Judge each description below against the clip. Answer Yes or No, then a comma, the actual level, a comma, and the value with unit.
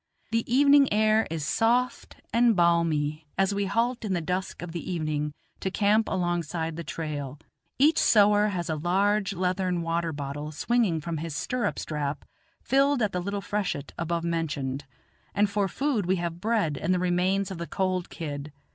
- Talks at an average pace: Yes, average, 175 wpm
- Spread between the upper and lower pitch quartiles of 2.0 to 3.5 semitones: No, average, 4.4 semitones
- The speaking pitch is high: No, medium, 180 Hz